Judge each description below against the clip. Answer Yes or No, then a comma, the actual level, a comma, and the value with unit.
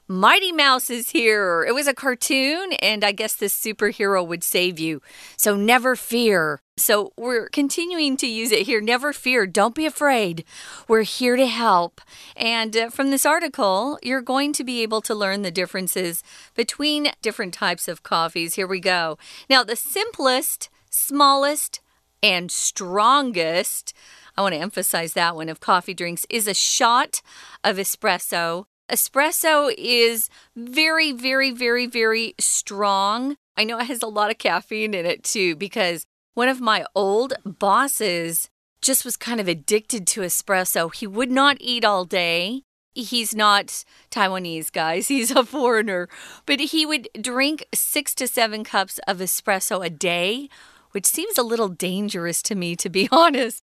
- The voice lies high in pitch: Yes, high, 220 Hz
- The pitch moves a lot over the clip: Yes, wide, 5.7 semitones